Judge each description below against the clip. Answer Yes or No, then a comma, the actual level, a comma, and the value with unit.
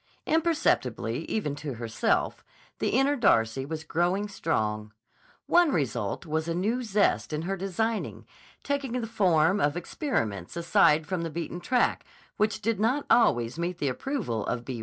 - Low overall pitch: No, medium, 175 Hz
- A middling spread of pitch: No, wide, 7.7 semitones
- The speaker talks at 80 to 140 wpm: No, average, 155 wpm